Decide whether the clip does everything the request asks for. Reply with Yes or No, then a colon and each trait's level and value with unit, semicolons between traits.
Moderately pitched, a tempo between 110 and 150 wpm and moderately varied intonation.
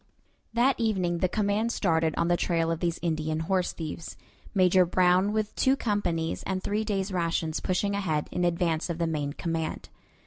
No: medium, 175 Hz; average, 175 wpm; average, 3.5 semitones